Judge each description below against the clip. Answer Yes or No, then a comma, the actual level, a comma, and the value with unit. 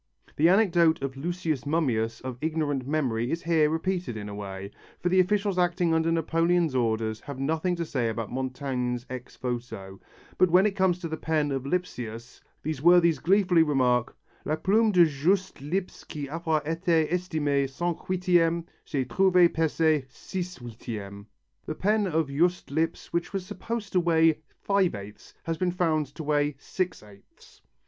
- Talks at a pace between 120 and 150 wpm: No, average, 165 wpm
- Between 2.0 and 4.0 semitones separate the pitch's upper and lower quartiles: No, average, 5.2 semitones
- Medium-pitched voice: Yes, medium, 160 Hz